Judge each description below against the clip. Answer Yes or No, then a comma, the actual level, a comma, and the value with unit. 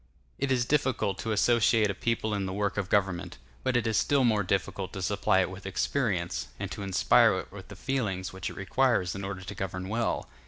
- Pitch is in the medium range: No, low, 100 Hz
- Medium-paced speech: No, fast, 220 wpm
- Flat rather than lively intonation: No, average, 3.7 semitones